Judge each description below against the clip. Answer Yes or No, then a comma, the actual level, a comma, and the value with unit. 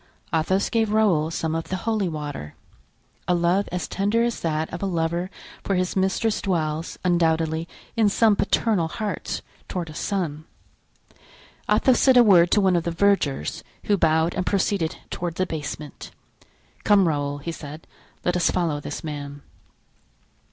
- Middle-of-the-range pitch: Yes, medium, 175 Hz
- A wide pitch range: No, average, 3.9 semitones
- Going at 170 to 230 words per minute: No, average, 160 wpm